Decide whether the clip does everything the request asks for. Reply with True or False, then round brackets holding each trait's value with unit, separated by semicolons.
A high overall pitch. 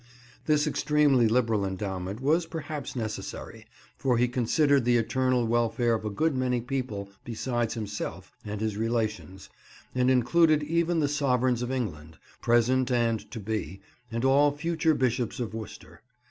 False (125 Hz)